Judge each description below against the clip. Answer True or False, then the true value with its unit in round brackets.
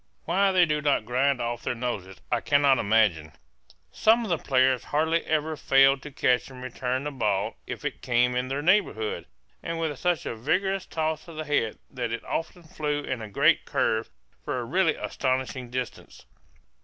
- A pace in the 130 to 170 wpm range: False (185 wpm)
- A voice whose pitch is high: False (135 Hz)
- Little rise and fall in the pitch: False (4.4 semitones)